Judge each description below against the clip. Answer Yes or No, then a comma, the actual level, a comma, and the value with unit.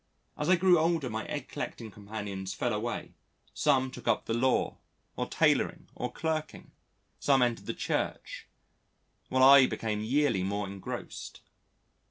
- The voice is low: Yes, low, 125 Hz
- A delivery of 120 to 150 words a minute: Yes, average, 145 wpm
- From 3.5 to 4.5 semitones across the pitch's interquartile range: No, average, 5.2 semitones